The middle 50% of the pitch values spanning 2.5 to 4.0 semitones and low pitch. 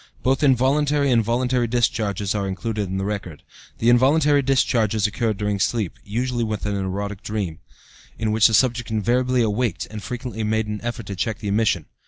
Yes: average, 3.3 semitones; low, 110 Hz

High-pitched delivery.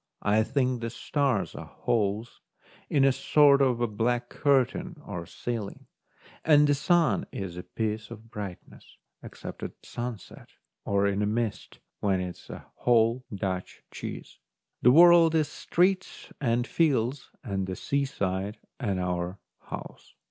No: low, 115 Hz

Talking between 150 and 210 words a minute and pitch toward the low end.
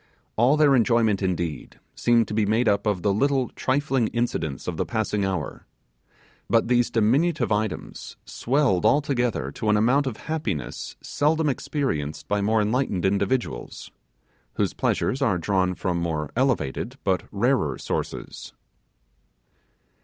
No: slow, 135 wpm; low, 110 Hz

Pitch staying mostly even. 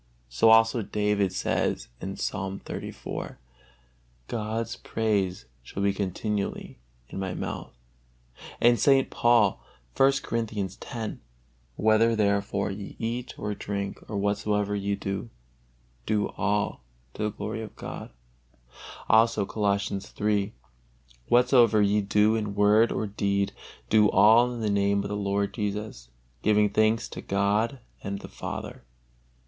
Yes: narrow, 1.9 semitones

